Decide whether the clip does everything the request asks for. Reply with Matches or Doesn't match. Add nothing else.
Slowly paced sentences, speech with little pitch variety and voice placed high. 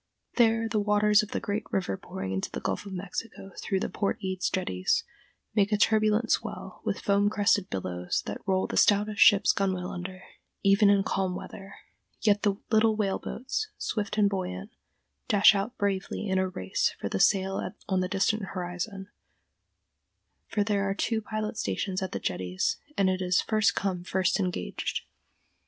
Doesn't match